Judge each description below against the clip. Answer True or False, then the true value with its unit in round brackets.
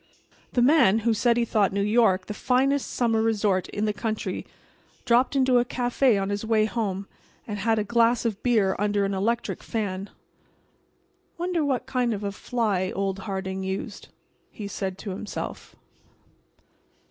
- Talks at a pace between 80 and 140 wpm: False (160 wpm)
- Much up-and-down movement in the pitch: False (3.3 semitones)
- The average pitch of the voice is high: True (215 Hz)